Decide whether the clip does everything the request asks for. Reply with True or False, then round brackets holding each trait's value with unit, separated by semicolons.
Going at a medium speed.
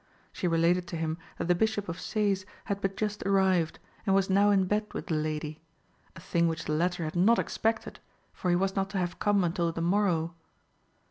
False (210 wpm)